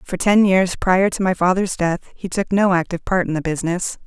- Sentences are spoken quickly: Yes, fast, 235 wpm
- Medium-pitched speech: Yes, medium, 180 Hz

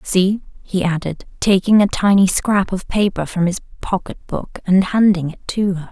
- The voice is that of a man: No, female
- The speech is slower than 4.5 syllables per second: No, 4.6 syllables/s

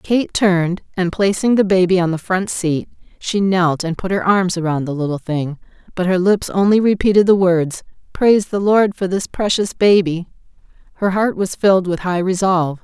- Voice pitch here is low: No, medium, 185 Hz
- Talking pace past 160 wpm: Yes, average, 190 wpm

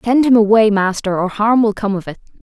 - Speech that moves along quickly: Yes, fast, 245 wpm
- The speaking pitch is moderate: No, high, 215 Hz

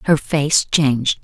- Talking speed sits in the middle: Yes, average, 145 wpm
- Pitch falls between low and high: Yes, medium, 145 Hz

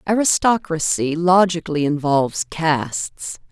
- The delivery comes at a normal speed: No, slow, 70 wpm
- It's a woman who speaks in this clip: Yes, female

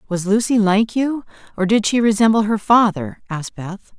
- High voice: Yes, high, 210 Hz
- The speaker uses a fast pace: No, average, 180 wpm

